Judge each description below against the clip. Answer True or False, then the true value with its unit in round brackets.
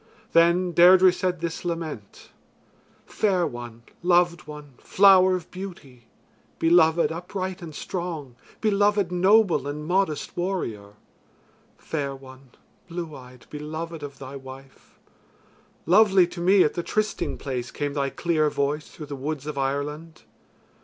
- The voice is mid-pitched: True (165 Hz)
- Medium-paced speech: False (130 wpm)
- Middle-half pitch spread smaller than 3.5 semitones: False (4.2 semitones)